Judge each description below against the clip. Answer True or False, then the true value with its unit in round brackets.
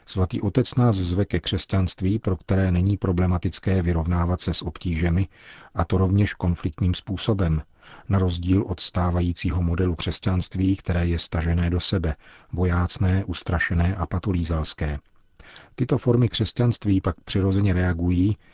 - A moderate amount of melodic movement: False (2.0 semitones)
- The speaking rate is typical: True (130 wpm)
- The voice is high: False (90 Hz)